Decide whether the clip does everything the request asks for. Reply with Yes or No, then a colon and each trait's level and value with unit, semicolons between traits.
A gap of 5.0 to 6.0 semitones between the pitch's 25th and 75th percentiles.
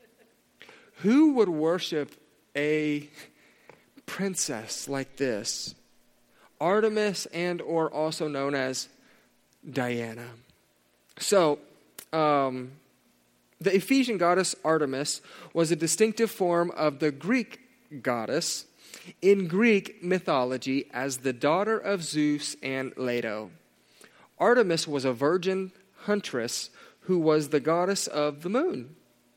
Yes: wide, 5.4 semitones